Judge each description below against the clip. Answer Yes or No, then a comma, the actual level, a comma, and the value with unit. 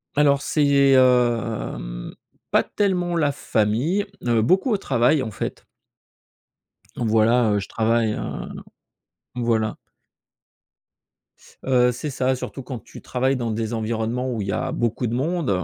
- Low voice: Yes, low, 125 Hz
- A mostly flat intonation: No, average, 3.7 semitones